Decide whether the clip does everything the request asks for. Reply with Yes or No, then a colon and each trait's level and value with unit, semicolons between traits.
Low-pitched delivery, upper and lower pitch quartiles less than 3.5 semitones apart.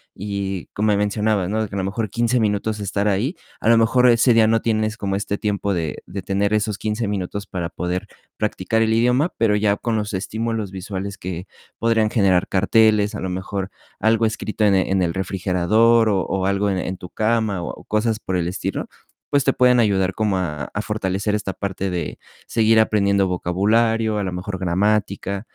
Yes: low, 105 Hz; narrow, 2.6 semitones